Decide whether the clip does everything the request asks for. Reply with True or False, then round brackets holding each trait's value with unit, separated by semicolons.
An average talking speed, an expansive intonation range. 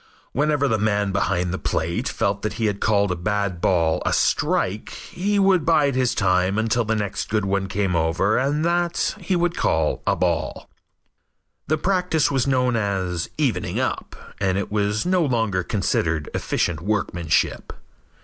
True (165 wpm; 6.8 semitones)